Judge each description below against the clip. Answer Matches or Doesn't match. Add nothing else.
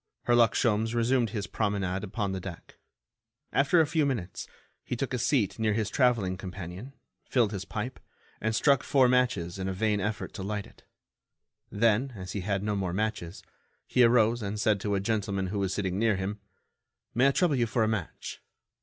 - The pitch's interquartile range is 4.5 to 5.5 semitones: Doesn't match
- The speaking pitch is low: Matches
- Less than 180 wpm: Doesn't match